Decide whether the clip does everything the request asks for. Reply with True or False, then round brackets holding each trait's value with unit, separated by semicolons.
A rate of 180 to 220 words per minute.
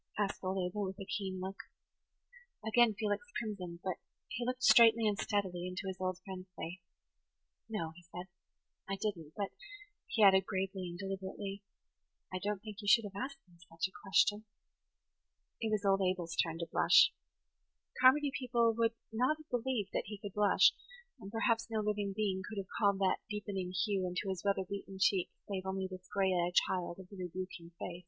True (190 wpm)